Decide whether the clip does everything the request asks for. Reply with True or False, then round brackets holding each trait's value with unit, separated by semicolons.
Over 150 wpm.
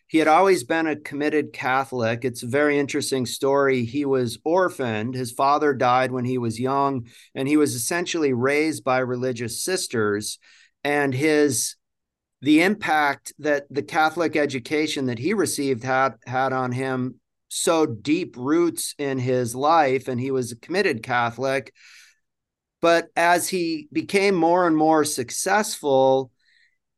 False (145 wpm)